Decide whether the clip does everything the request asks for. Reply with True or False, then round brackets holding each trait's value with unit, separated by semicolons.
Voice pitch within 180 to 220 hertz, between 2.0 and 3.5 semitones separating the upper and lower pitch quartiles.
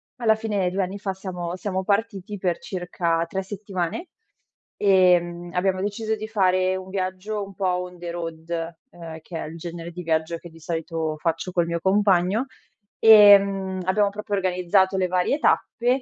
True (185 Hz; 2.6 semitones)